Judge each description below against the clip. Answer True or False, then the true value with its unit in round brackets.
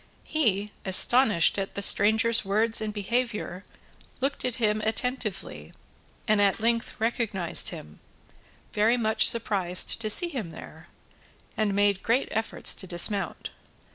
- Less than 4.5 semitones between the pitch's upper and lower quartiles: True (2.8 semitones)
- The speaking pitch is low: False (215 Hz)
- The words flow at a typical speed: False (130 wpm)